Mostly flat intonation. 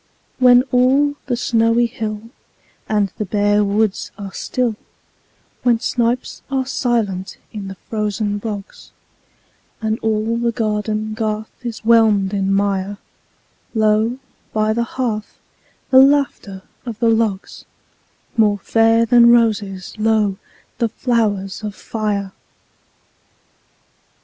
Yes: narrow, 2.3 semitones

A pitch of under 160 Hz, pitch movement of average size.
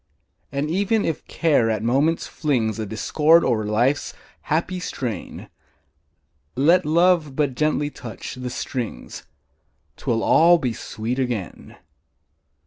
No: medium, 140 Hz; wide, 5.8 semitones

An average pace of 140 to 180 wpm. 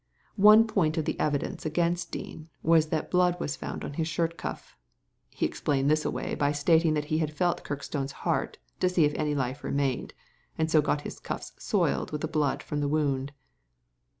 No: average, 195 wpm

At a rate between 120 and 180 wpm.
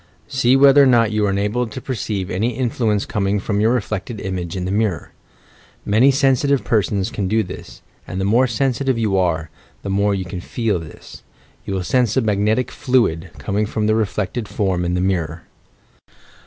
No: average, 190 wpm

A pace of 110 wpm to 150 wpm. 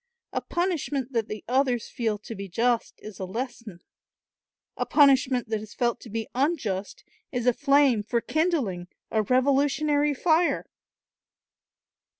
Yes: average, 140 wpm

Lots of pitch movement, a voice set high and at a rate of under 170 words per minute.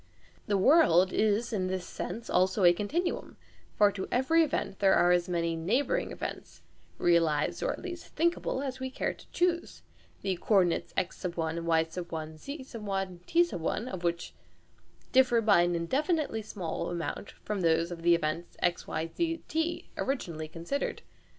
Yes: wide, 7.5 semitones; high, 195 Hz; average, 155 wpm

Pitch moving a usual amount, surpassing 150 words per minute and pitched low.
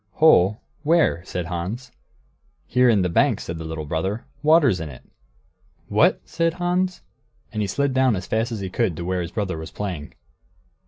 No: wide, 7.3 semitones; average, 180 wpm; low, 100 Hz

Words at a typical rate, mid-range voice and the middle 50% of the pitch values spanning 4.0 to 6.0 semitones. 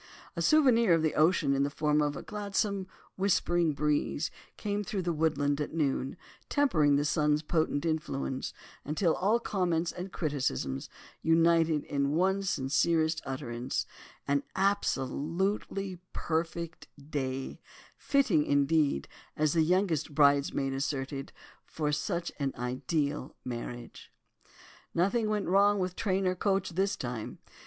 No: slow, 130 wpm; medium, 160 Hz; average, 4.8 semitones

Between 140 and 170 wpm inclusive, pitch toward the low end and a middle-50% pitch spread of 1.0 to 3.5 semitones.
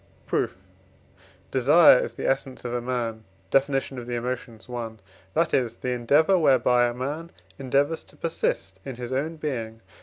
Yes: average, 160 wpm; low, 125 Hz; average, 2.9 semitones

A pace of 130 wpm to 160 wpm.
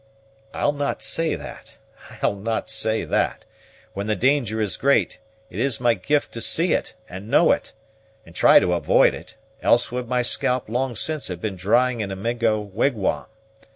No: average, 185 wpm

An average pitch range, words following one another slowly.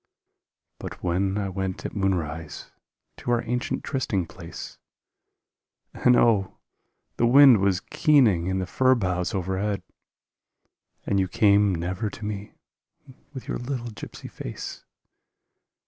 Yes: average, 4.3 semitones; slow, 125 wpm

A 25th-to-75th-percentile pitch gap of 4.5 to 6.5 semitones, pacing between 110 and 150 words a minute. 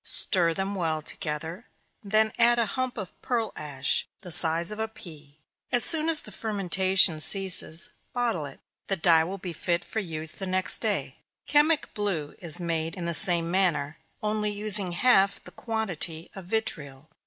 No: average, 4.8 semitones; average, 175 wpm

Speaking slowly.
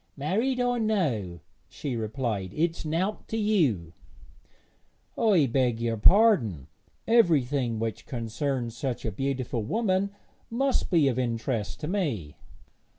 Yes: slow, 120 wpm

